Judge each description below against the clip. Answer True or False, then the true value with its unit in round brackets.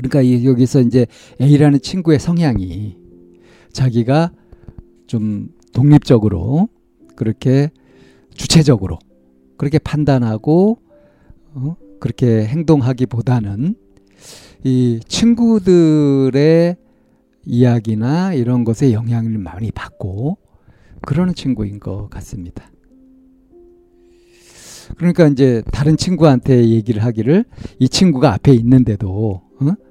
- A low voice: True (130 Hz)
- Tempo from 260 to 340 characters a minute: False (225 characters per minute)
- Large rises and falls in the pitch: True (6.5 semitones)